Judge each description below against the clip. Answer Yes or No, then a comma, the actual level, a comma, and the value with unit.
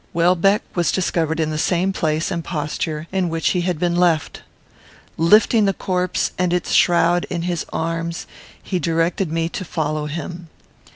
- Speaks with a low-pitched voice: No, medium, 170 Hz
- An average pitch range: No, narrow, 1.8 semitones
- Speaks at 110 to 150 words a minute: No, average, 165 wpm